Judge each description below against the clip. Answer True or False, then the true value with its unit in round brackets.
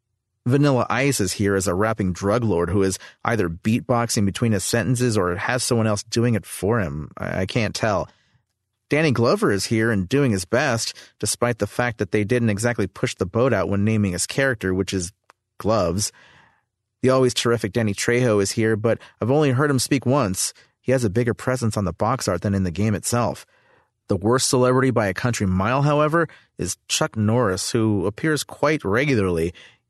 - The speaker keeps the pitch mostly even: False (3.8 semitones)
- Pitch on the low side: True (115 Hz)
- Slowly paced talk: False (195 wpm)